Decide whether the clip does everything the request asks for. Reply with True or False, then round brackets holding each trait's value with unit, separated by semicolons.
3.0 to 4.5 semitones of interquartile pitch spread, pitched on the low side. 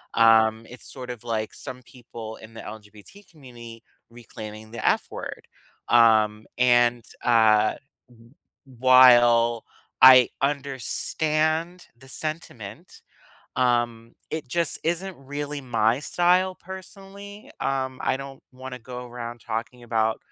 True (3.7 semitones; 125 Hz)